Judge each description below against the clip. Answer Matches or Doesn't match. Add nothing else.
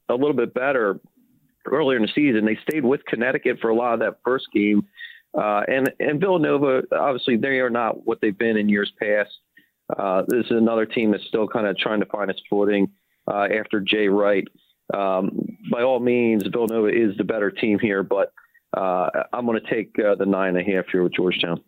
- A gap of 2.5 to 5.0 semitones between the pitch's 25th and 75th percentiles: Matches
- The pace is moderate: Doesn't match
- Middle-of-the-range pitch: Doesn't match